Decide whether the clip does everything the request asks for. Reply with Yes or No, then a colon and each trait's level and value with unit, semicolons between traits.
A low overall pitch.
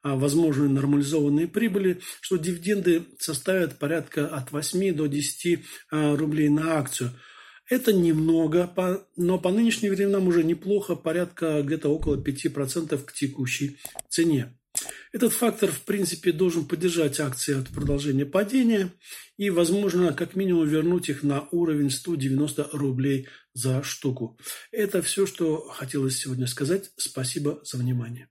No: medium, 160 Hz